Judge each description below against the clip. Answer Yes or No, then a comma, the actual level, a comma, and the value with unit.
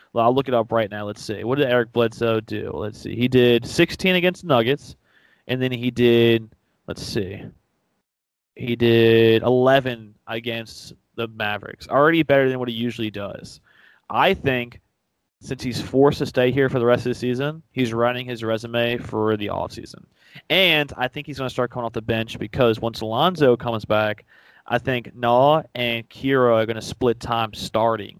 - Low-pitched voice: Yes, low, 120 Hz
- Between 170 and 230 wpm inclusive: Yes, average, 190 wpm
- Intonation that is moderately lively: No, narrow, 2.3 semitones